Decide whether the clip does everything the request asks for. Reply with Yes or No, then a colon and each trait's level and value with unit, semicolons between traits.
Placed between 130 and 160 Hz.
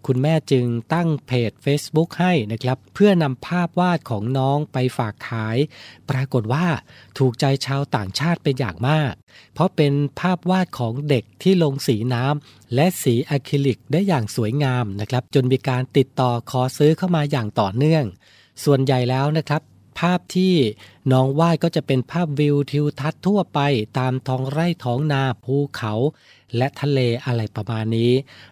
Yes: low, 135 Hz